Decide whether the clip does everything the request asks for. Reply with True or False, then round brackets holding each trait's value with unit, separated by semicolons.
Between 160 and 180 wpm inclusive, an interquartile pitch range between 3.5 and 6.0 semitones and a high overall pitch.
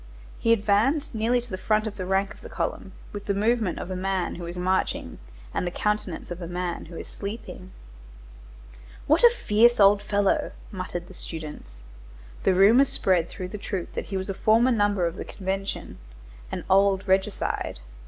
False (175 wpm; 2.9 semitones; 195 Hz)